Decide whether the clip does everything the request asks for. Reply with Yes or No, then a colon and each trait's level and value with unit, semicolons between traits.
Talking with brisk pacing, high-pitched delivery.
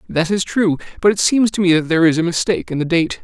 No: fast, 295 wpm; medium, 180 Hz